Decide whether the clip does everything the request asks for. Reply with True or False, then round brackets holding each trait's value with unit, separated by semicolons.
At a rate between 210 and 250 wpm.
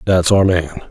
False (200 wpm)